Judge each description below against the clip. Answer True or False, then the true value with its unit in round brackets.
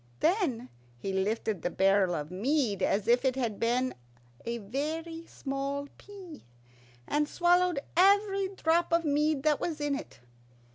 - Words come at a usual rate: True (145 wpm)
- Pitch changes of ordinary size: False (6.6 semitones)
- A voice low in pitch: False (280 Hz)